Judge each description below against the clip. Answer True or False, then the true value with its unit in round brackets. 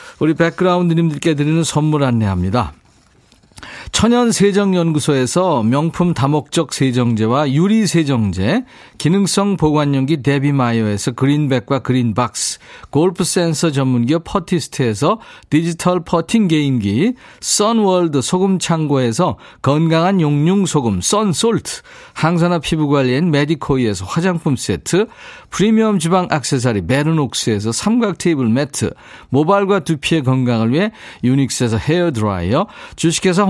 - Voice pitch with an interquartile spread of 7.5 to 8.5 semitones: False (5.9 semitones)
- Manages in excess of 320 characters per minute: False (310 characters per minute)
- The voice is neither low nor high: True (155 Hz)